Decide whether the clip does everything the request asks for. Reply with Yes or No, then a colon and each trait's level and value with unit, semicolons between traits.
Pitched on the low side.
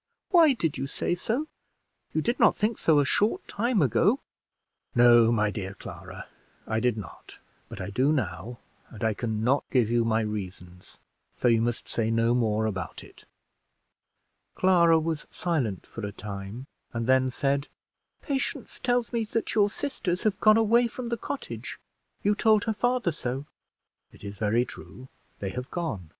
Yes: low, 130 Hz